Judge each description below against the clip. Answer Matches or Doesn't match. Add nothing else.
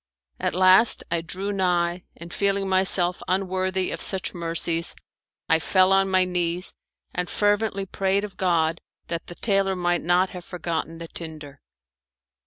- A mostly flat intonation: Matches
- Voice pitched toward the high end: Doesn't match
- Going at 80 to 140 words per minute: Doesn't match